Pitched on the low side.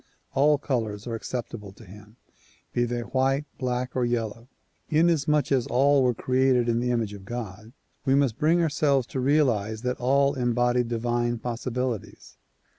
Yes: low, 125 Hz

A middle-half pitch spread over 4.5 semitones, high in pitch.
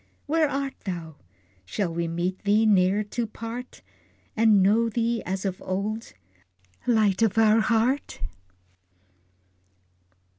No: average, 3.4 semitones; high, 215 Hz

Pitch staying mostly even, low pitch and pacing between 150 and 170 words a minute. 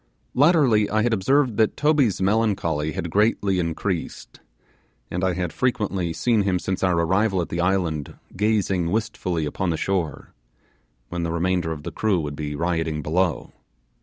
No: average, 4.2 semitones; very low, 95 Hz; average, 160 wpm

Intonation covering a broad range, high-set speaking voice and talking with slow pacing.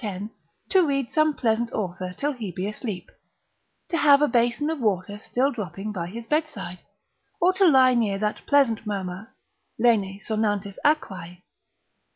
No: wide, 6.2 semitones; high, 225 Hz; average, 150 wpm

